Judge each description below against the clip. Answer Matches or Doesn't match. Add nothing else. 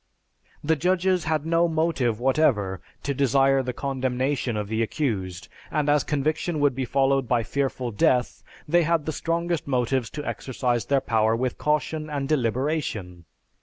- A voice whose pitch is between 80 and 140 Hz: Matches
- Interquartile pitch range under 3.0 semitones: Doesn't match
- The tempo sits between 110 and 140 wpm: Doesn't match